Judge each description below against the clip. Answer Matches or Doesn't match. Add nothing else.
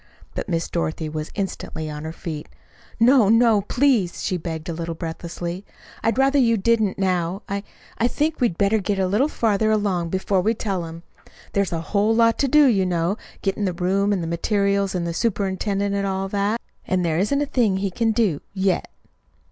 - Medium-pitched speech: Doesn't match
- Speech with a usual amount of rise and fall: Matches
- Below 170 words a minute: Doesn't match